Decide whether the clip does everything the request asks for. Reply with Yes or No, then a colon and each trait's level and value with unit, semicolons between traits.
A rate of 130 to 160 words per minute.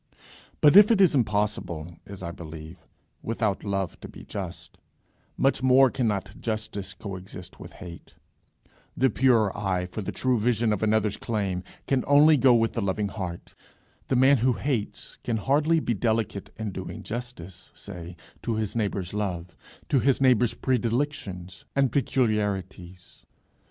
Yes: average, 150 wpm